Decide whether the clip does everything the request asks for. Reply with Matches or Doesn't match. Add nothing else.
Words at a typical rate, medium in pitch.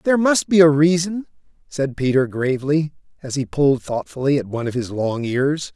Matches